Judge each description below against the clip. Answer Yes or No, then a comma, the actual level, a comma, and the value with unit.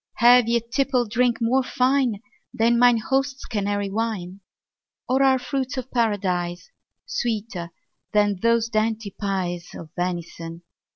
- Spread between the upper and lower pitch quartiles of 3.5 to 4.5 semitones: Yes, average, 4.1 semitones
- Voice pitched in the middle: No, high, 225 Hz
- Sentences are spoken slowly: Yes, slow, 125 wpm